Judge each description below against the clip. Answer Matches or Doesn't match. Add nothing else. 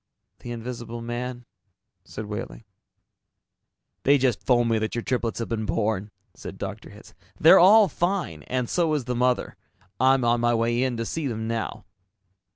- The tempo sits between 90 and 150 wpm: Doesn't match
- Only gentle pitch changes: Matches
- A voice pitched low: Matches